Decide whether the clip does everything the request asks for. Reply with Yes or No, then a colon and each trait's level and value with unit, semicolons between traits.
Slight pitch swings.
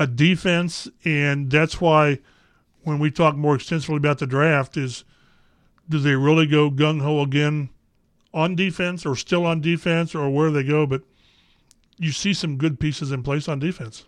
Yes: narrow, 2.3 semitones